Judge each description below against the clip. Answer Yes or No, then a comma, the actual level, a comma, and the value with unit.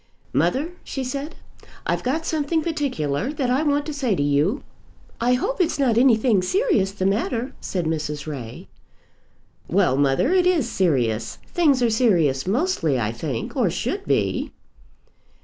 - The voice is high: Yes, high, 230 Hz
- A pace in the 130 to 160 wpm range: Yes, average, 150 wpm